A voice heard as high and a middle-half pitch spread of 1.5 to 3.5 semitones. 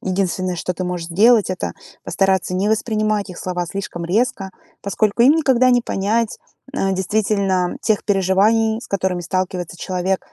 Yes: high, 195 Hz; average, 2.9 semitones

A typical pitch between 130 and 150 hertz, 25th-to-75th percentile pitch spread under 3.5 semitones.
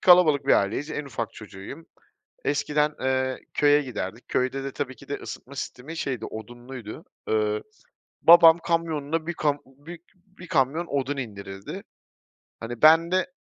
No: medium, 140 Hz; average, 4.7 semitones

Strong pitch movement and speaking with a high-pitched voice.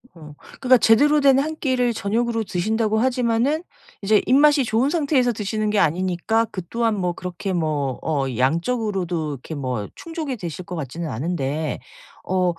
Yes: wide, 6.7 semitones; high, 210 Hz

